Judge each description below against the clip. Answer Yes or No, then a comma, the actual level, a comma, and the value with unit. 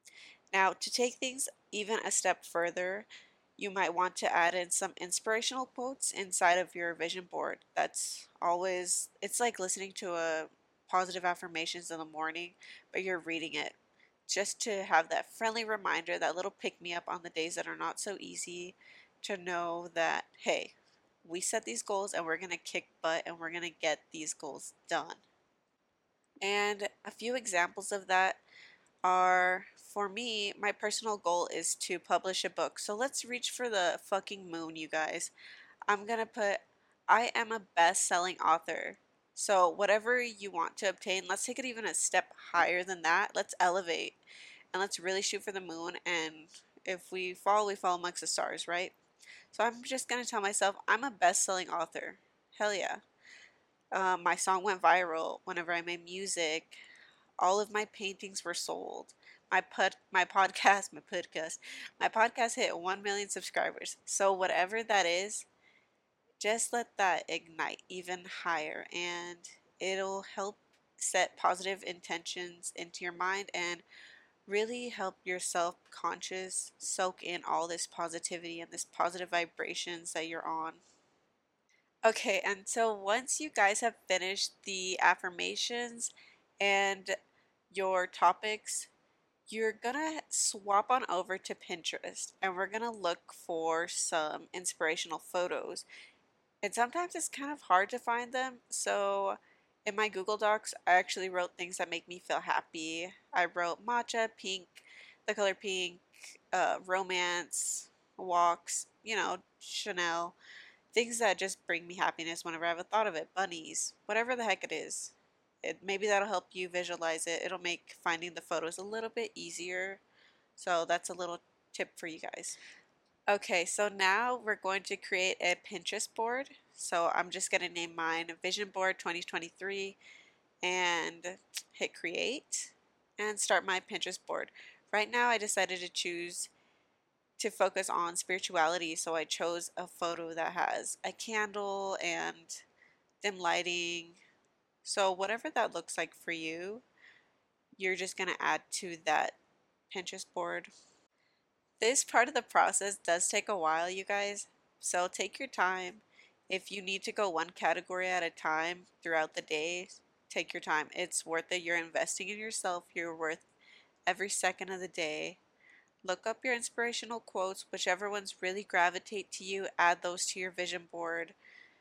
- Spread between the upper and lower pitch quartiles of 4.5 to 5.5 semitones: No, average, 2.9 semitones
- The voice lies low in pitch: No, medium, 185 Hz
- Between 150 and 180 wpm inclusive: Yes, average, 160 wpm